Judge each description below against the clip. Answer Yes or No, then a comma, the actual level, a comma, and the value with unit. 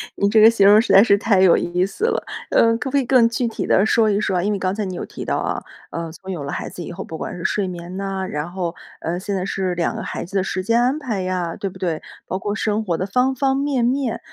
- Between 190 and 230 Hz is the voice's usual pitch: Yes, high, 195 Hz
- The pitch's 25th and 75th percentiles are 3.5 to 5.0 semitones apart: Yes, average, 4.0 semitones